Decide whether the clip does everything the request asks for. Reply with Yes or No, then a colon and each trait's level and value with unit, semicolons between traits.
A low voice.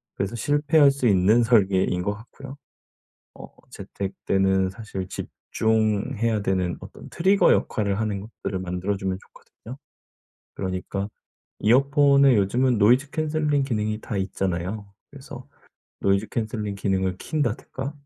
Yes: low, 110 Hz